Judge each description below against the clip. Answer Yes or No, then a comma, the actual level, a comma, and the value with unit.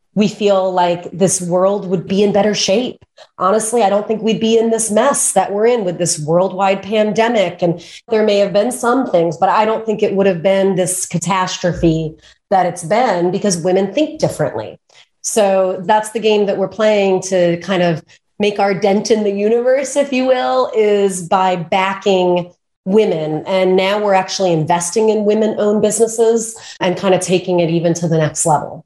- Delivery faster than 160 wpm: Yes, average, 190 wpm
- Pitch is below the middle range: No, high, 195 Hz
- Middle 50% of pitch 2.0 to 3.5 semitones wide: Yes, average, 3.0 semitones